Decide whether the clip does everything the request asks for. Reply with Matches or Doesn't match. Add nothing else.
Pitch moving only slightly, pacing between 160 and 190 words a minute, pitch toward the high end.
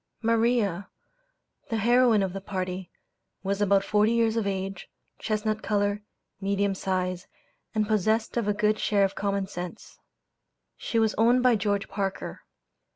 Doesn't match